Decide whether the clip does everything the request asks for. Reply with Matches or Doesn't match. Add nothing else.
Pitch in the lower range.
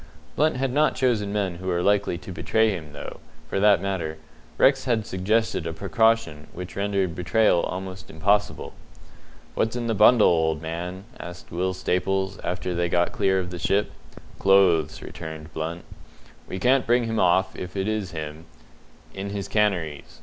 Matches